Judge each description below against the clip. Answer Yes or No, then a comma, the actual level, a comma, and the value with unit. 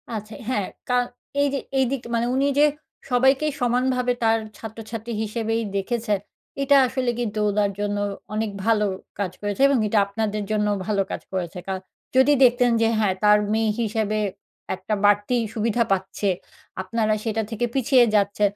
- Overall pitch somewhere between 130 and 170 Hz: No, high, 220 Hz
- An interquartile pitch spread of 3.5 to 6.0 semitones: No, average, 3.0 semitones